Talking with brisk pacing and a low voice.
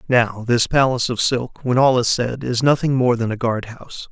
Yes: fast, 235 wpm; low, 120 Hz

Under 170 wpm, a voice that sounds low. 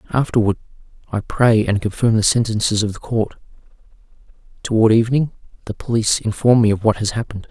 Yes: average, 160 wpm; low, 110 Hz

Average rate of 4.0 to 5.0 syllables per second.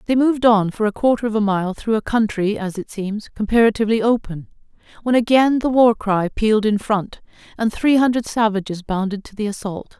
No: 5.5 syllables/s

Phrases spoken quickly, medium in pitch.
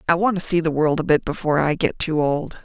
Yes: fast, 295 wpm; medium, 160 Hz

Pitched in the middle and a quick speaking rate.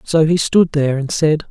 Yes: medium, 155 Hz; fast, 240 wpm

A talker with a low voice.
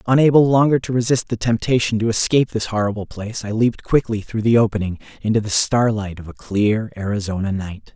Yes: low, 110 Hz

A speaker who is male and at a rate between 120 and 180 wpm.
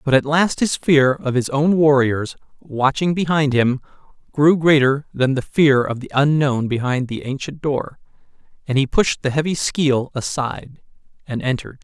Yes: male; average, 165 wpm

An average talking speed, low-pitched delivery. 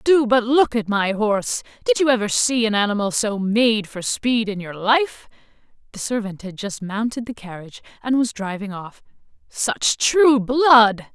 No: average, 180 wpm; high, 225 Hz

